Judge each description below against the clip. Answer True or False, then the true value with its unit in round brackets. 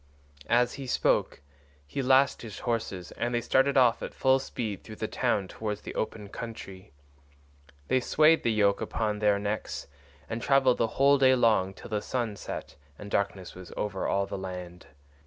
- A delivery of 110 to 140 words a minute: False (175 wpm)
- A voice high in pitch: False (110 Hz)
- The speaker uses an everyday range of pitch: True (4.0 semitones)